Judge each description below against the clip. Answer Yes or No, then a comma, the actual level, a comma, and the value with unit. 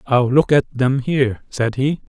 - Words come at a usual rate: Yes, average, 190 wpm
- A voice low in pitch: Yes, low, 130 Hz